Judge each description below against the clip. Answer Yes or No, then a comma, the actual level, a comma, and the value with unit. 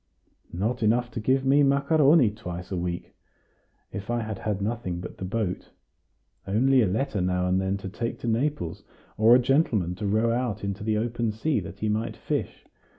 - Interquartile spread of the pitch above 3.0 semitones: Yes, average, 4.1 semitones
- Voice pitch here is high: No, low, 110 Hz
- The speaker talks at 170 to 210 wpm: Yes, average, 190 wpm